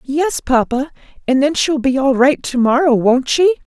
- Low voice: No, very high, 265 Hz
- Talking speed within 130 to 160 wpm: No, average, 190 wpm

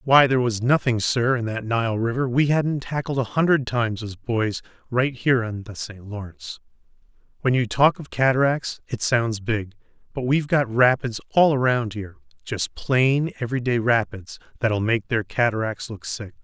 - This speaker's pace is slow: No, average, 185 wpm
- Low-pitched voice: Yes, low, 120 Hz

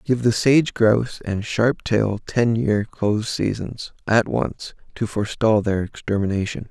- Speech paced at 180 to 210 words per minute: No, average, 150 wpm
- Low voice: Yes, low, 110 Hz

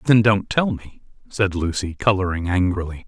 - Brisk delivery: No, average, 155 wpm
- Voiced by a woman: No, male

